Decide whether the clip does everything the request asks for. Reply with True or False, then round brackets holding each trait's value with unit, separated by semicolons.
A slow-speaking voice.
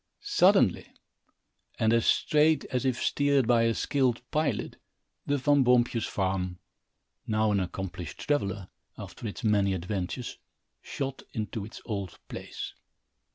True (125 wpm)